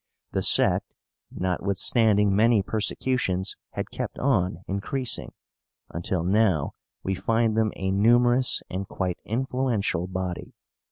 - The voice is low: Yes, low, 100 Hz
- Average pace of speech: No, slow, 110 wpm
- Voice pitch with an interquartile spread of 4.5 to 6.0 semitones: No, average, 3.8 semitones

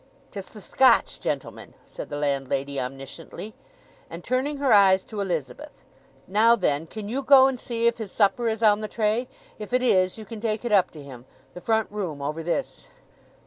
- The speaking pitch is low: No, high, 210 Hz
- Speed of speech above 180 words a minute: Yes, average, 190 wpm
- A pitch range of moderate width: No, wide, 6.0 semitones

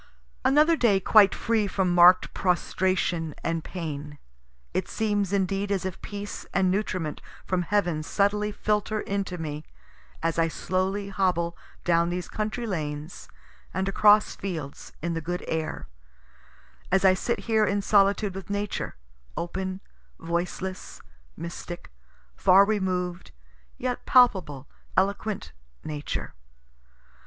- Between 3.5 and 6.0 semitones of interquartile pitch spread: No, average, 3.0 semitones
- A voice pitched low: No, high, 190 Hz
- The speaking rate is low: Yes, slow, 120 wpm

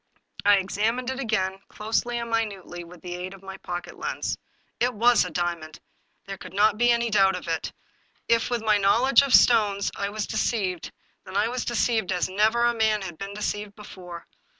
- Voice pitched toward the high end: Yes, high, 205 Hz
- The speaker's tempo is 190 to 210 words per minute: Yes, average, 195 wpm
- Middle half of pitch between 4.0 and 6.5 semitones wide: No, average, 3.5 semitones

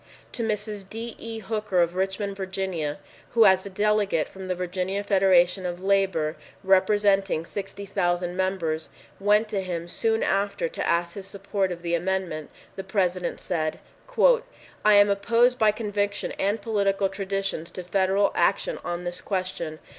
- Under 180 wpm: Yes, average, 150 wpm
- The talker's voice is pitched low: No, high, 195 Hz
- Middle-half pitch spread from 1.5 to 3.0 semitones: Yes, narrow, 2.4 semitones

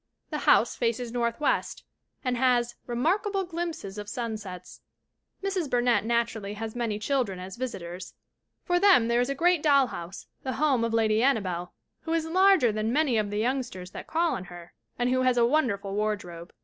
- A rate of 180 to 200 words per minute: Yes, average, 185 wpm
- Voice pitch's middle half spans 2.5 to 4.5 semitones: No, average, 5.0 semitones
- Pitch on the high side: Yes, high, 235 Hz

